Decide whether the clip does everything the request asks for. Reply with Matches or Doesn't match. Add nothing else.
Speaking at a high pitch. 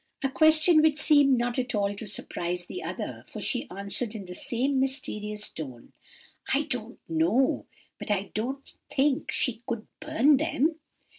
Matches